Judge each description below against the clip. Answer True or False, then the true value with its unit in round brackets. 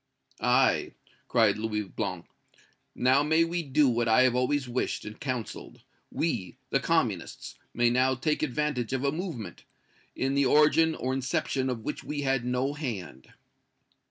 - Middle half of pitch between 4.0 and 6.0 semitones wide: False (3.6 semitones)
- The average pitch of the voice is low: True (130 Hz)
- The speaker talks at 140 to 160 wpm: True (155 wpm)